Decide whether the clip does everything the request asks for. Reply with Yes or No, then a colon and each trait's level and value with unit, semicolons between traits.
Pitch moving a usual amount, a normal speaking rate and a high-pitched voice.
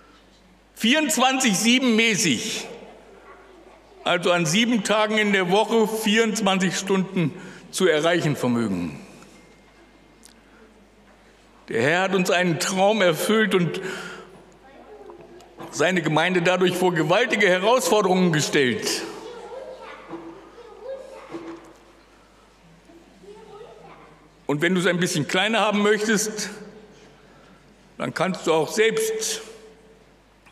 No: average, 3.9 semitones; slow, 85 wpm; high, 210 Hz